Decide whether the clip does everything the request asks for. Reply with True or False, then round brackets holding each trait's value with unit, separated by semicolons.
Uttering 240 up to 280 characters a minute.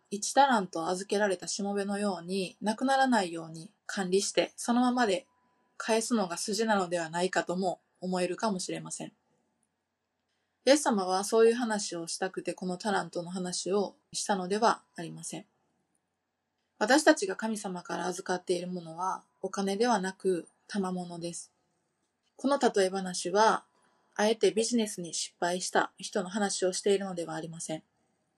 False (325 characters per minute)